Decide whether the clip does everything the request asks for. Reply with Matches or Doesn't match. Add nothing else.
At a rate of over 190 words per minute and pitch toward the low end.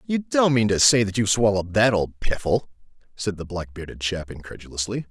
Matches